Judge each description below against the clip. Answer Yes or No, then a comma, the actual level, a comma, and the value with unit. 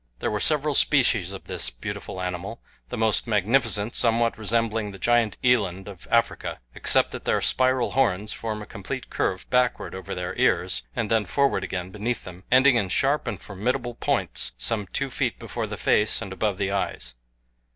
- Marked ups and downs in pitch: No, average, 3.8 semitones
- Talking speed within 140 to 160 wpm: No, average, 180 wpm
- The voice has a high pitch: No, low, 110 Hz